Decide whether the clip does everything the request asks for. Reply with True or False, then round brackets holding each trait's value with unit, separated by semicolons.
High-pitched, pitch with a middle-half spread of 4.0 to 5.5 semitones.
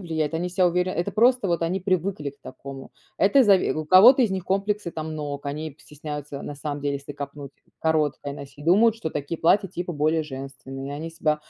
False (155 Hz; 4.3 semitones)